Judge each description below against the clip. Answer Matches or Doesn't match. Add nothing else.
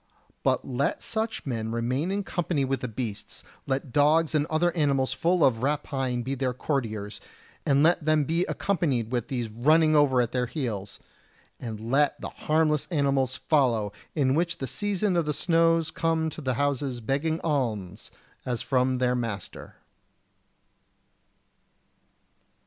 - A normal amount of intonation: Matches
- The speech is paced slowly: Doesn't match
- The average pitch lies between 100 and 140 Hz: Matches